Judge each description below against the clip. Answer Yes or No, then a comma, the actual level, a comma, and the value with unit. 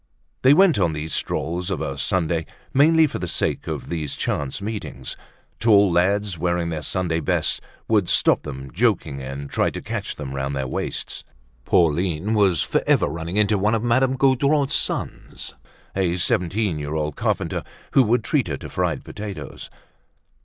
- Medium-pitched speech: No, very low, 90 Hz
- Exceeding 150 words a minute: Yes, average, 165 wpm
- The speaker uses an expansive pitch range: Yes, wide, 5.8 semitones